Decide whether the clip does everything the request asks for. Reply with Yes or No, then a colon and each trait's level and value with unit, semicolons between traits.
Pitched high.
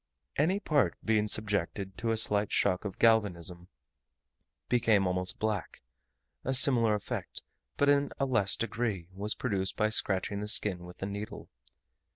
No: low, 105 Hz